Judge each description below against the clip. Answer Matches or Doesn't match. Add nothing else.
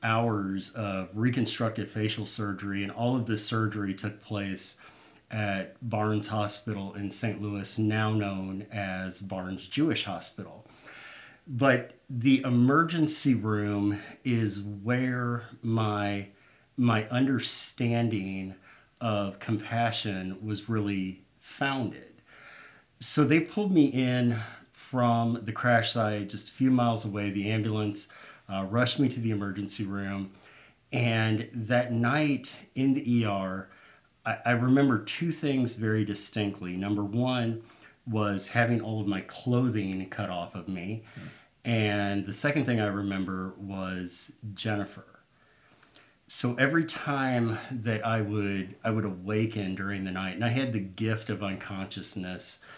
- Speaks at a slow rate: Matches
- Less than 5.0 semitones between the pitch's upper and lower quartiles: Matches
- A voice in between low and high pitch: Doesn't match